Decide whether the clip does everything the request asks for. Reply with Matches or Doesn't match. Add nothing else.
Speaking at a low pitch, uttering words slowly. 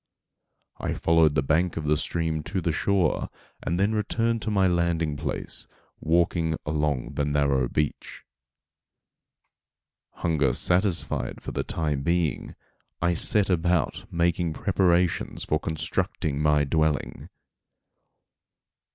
Matches